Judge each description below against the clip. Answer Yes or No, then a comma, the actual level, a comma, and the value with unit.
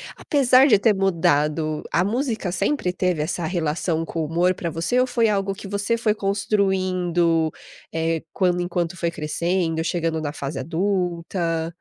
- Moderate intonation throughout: Yes, average, 3.3 semitones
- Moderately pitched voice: Yes, medium, 175 Hz